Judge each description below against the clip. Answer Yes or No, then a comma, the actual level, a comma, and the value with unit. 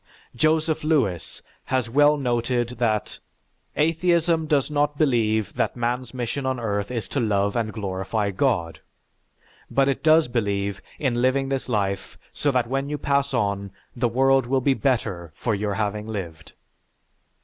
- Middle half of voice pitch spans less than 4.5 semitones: No, average, 5.0 semitones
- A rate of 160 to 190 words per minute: No, average, 150 wpm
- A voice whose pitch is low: Yes, low, 120 Hz